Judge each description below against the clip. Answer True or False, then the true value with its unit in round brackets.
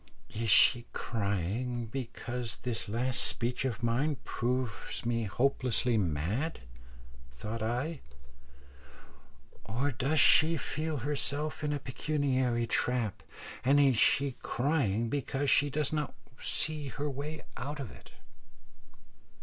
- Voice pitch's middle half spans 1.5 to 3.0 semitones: False (3.7 semitones)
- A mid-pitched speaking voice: False (125 Hz)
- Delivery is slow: True (115 wpm)